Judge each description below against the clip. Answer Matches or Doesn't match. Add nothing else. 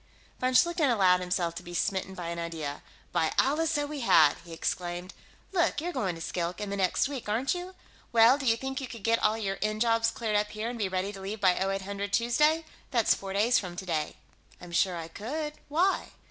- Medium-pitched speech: Doesn't match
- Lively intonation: Matches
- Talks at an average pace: Doesn't match